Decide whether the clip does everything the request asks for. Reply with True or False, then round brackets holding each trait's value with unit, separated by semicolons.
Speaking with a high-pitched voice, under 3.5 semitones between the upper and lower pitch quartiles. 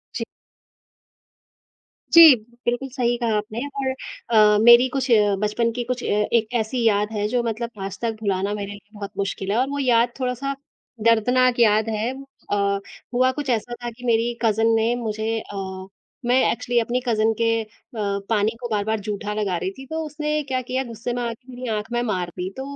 True (230 Hz; 3.0 semitones)